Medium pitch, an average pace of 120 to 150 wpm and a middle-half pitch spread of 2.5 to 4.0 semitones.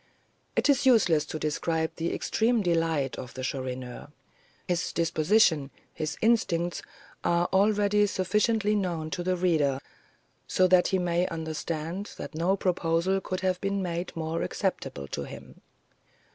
Yes: medium, 175 Hz; average, 140 wpm; average, 3.3 semitones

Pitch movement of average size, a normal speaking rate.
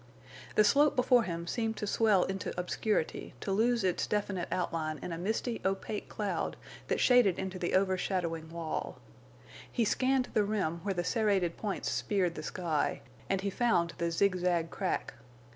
Yes: average, 3.7 semitones; average, 165 wpm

